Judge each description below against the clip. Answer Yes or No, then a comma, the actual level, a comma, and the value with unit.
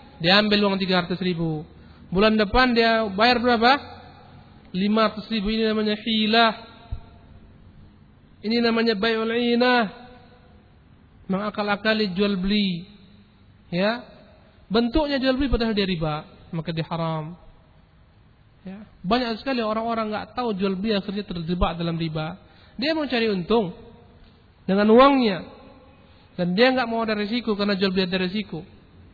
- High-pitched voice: Yes, high, 210 Hz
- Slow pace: No, average, 130 wpm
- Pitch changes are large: No, average, 4.2 semitones